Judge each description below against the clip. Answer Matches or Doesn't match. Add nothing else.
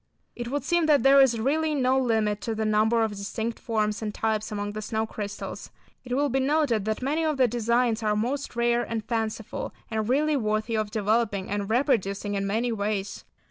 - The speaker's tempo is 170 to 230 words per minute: Matches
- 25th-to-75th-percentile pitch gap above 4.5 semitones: Doesn't match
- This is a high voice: Matches